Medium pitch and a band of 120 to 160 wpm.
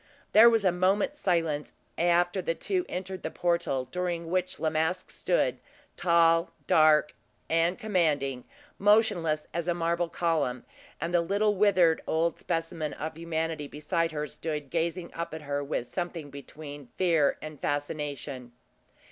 Yes: medium, 165 Hz; average, 145 wpm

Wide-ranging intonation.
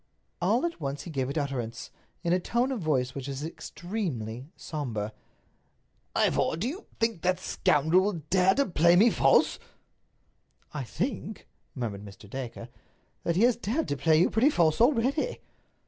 Yes: wide, 8.3 semitones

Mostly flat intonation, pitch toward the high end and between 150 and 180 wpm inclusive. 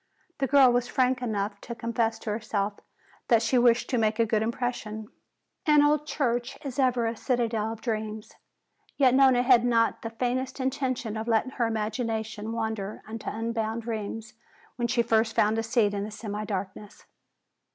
Yes: narrow, 2.2 semitones; high, 230 Hz; average, 170 wpm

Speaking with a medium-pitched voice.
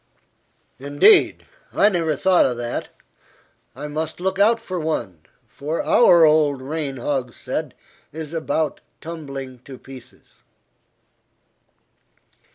Yes: medium, 150 Hz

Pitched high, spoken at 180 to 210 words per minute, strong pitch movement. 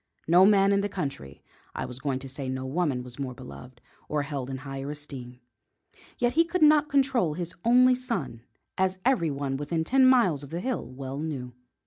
No: medium, 150 Hz; average, 190 wpm; wide, 8.0 semitones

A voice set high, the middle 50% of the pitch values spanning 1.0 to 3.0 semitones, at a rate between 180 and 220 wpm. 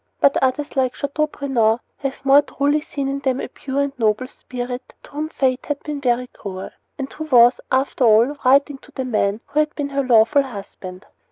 Yes: very high, 265 Hz; narrow, 2.6 semitones; average, 195 wpm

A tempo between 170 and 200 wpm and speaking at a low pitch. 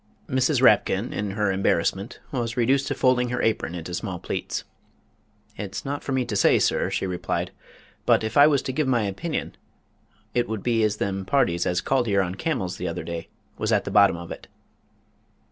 Yes: average, 195 wpm; low, 110 Hz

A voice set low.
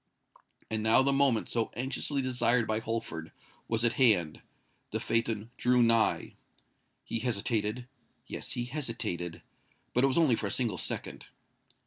Yes: low, 115 Hz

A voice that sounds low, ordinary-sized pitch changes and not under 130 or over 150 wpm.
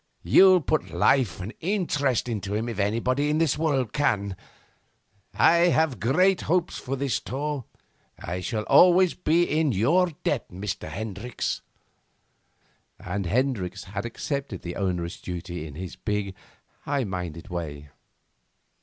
No: low, 115 Hz; wide, 7.6 semitones; slow, 135 wpm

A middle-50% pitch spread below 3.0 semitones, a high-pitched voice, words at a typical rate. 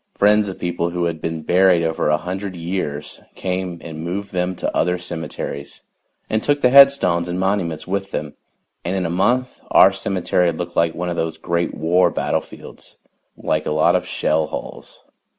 No: narrow, 2.5 semitones; very low, 90 Hz; average, 180 wpm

